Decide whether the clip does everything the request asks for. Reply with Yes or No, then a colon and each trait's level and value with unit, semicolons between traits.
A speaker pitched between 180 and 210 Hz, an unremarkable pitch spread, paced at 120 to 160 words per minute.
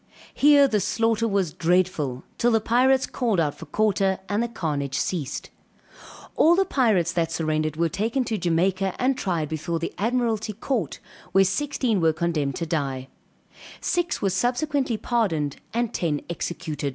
No: high, 190 Hz; wide, 6.3 semitones; average, 155 wpm